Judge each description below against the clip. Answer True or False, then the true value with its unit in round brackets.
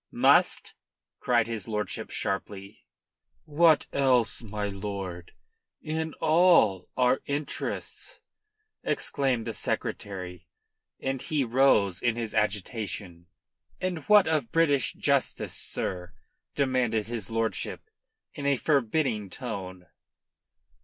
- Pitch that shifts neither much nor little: False (5.8 semitones)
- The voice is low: True (115 Hz)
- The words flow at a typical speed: False (100 wpm)